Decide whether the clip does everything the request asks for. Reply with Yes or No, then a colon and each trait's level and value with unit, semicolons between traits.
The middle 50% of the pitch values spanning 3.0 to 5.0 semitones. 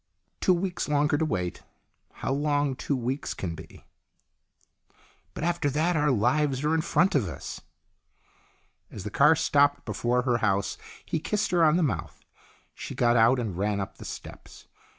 No: wide, 5.4 semitones